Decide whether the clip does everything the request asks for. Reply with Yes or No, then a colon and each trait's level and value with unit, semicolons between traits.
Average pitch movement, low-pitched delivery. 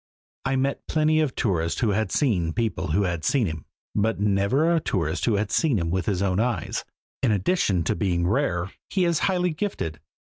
No: wide, 7.5 semitones; low, 105 Hz